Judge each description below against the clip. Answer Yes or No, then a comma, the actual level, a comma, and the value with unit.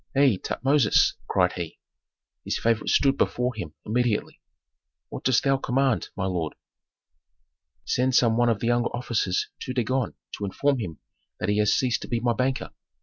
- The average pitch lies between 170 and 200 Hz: No, low, 120 Hz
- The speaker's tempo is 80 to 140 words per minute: No, average, 165 wpm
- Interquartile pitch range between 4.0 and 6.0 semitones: No, average, 3.6 semitones